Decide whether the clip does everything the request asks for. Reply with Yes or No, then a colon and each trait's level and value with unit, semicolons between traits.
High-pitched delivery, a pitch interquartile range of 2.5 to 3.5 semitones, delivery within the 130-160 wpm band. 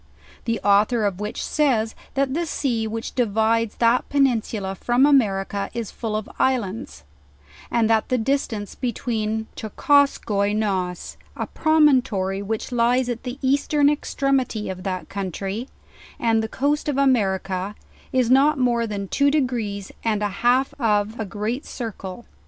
No: high, 225 Hz; average, 4.1 semitones; average, 145 wpm